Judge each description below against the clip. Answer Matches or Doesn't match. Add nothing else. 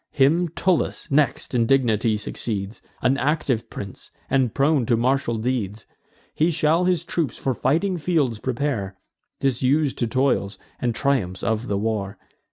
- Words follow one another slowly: Doesn't match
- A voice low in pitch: Matches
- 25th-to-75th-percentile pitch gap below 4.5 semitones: Doesn't match